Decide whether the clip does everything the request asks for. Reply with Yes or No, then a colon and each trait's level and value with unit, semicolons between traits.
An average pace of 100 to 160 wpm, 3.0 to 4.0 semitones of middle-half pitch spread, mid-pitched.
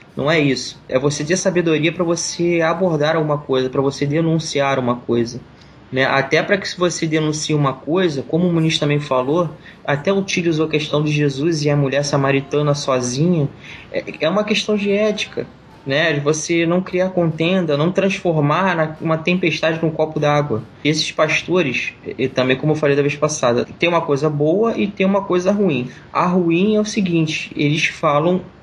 No: average, 180 wpm; average, 3.5 semitones; medium, 155 Hz